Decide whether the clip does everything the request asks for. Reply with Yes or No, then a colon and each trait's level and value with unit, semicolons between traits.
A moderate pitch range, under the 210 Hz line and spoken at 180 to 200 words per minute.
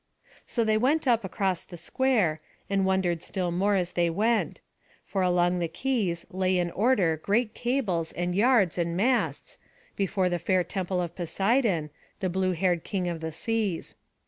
No: average, 3.8 semitones; medium, 185 Hz; average, 170 wpm